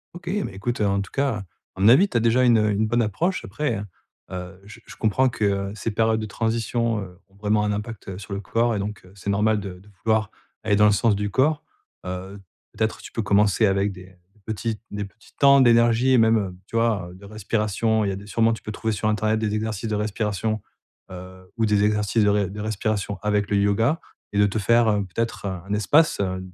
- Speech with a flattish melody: Yes, narrow, 2.2 semitones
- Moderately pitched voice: No, low, 105 Hz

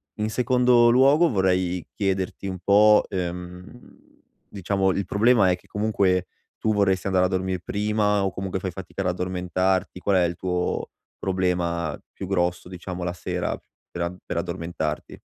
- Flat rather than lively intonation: Yes, narrow, 2.2 semitones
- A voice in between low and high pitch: No, very low, 95 Hz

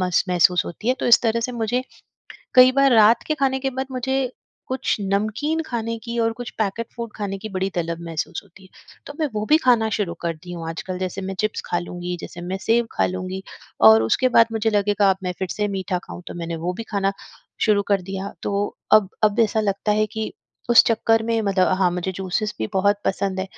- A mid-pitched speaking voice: No, high, 205 Hz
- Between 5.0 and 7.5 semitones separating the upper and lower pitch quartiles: No, average, 3.6 semitones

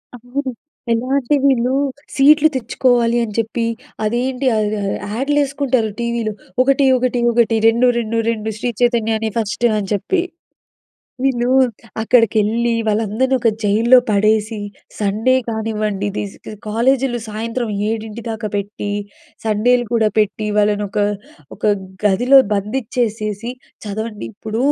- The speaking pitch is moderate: No, high, 230 Hz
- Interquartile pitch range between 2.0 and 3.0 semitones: Yes, narrow, 2.6 semitones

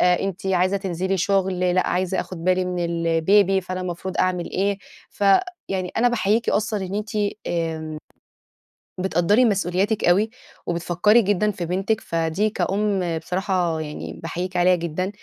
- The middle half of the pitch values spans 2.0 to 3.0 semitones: Yes, narrow, 2.4 semitones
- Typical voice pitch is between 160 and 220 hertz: Yes, medium, 185 Hz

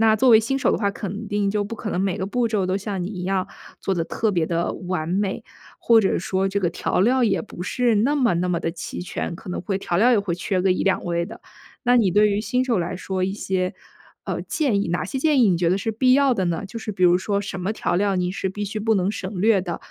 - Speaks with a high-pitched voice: Yes, high, 195 Hz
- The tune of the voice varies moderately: Yes, average, 3.3 semitones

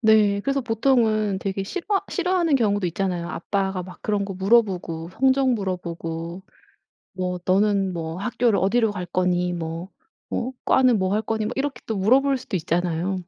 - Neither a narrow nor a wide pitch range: Yes, average, 4.3 semitones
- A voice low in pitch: No, high, 200 Hz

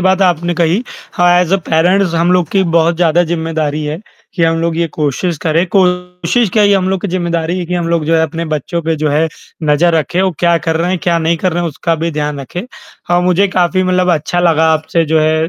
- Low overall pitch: No, medium, 170 Hz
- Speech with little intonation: Yes, narrow, 2.0 semitones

